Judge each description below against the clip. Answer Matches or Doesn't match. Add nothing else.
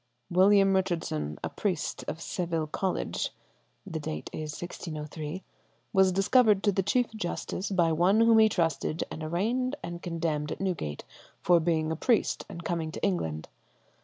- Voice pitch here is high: Doesn't match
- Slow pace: Doesn't match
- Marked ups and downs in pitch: Doesn't match